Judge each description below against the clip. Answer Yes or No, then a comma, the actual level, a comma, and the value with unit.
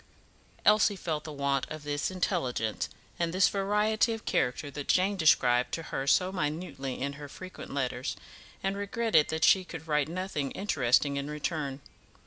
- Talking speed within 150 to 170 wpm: Yes, average, 160 wpm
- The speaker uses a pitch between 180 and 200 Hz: No, medium, 155 Hz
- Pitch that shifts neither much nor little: Yes, average, 5.0 semitones